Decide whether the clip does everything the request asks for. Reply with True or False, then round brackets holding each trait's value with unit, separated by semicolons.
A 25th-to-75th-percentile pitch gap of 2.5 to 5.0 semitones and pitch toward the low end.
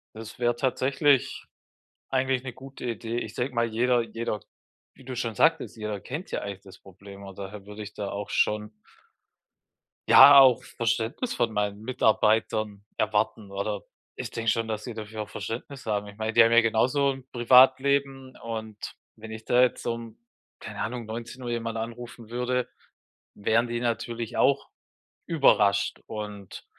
True (2.8 semitones; 115 Hz)